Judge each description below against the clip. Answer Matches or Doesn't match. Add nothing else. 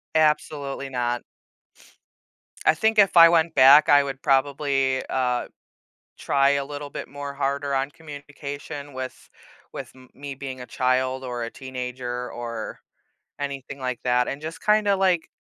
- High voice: Doesn't match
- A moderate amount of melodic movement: Doesn't match